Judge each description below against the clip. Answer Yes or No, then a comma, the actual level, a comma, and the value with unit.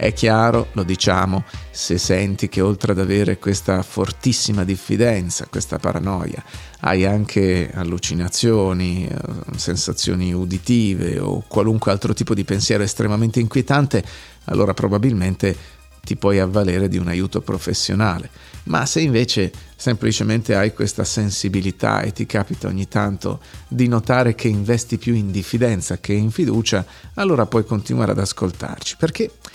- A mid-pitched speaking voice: No, low, 100 Hz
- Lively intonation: No, average, 3.3 semitones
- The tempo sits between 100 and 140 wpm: Yes, average, 130 wpm